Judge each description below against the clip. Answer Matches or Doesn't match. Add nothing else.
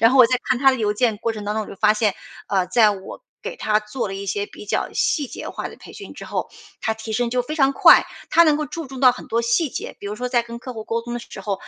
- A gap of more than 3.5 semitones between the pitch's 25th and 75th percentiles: Doesn't match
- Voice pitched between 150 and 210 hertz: Doesn't match